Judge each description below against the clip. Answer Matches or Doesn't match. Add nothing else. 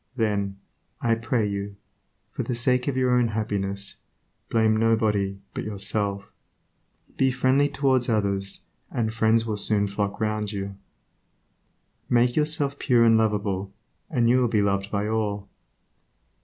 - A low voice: Matches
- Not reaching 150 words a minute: Matches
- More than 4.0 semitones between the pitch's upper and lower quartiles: Doesn't match